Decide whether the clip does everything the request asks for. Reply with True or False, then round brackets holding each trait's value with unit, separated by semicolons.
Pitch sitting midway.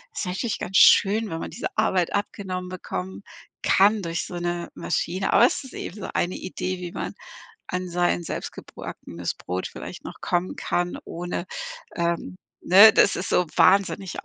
True (180 Hz)